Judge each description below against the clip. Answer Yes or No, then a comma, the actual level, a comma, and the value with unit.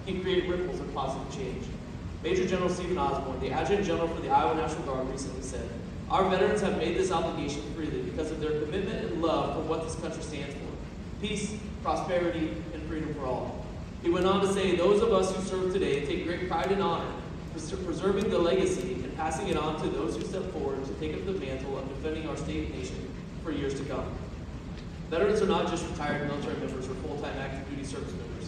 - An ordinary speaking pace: No, fast, 215 wpm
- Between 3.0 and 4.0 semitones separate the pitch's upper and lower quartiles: No, average, 4.6 semitones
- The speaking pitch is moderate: Yes, medium, 165 Hz